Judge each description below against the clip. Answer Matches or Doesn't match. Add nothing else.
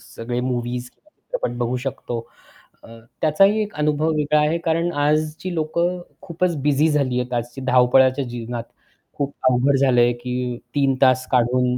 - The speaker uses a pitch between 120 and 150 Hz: Matches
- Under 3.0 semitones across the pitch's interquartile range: Doesn't match